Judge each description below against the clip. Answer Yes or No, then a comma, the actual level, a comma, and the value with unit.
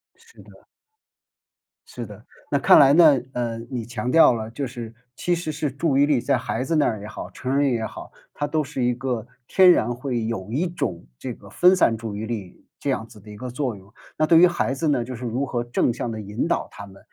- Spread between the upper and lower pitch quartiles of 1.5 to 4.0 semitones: No, average, 4.4 semitones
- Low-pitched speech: Yes, low, 125 Hz